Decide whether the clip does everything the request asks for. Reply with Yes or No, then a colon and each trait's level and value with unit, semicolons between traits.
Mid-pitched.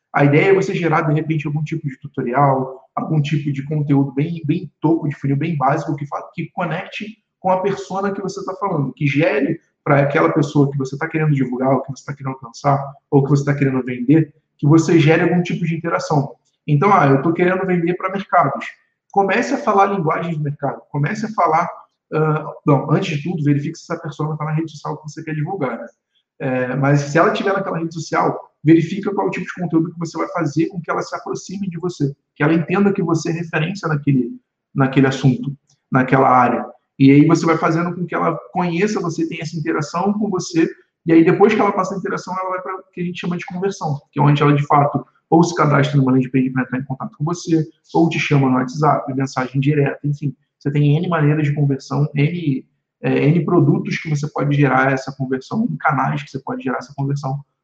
Yes: medium, 155 Hz